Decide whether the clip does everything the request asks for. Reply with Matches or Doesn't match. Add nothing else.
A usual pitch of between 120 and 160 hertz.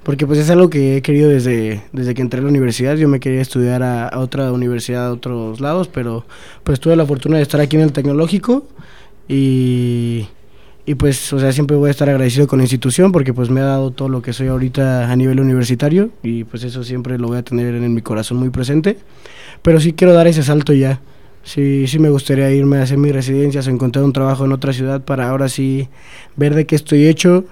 Matches